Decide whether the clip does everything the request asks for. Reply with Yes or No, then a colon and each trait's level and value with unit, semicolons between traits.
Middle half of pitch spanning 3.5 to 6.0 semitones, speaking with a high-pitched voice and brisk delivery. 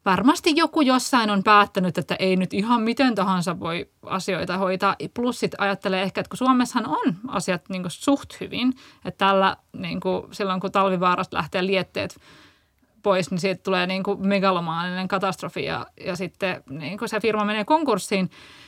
No: average, 2.9 semitones; high, 195 Hz; fast, 170 wpm